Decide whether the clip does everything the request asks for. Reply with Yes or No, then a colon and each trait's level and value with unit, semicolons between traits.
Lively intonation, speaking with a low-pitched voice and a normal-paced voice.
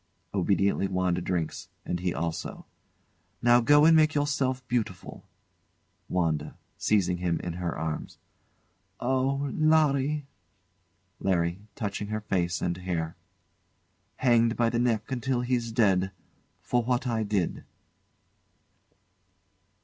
No: wide, 6.0 semitones; low, 110 Hz; slow, 110 wpm